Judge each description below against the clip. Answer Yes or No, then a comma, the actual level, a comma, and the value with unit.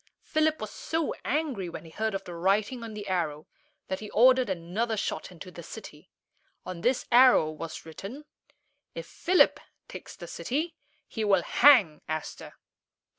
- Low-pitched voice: No, high, 215 Hz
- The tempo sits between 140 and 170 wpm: Yes, average, 160 wpm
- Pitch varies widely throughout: Yes, wide, 6.8 semitones